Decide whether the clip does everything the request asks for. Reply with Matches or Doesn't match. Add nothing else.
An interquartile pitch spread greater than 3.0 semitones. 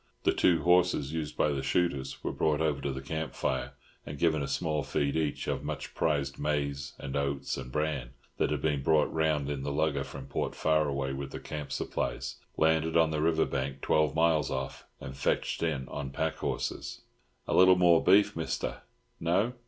Doesn't match